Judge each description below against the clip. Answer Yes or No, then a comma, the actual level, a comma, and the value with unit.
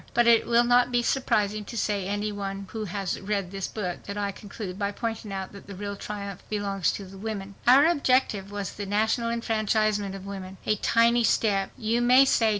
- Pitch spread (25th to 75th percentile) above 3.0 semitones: No, average, 2.7 semitones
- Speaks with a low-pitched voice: No, high, 205 Hz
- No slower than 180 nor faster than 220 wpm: Yes, average, 200 wpm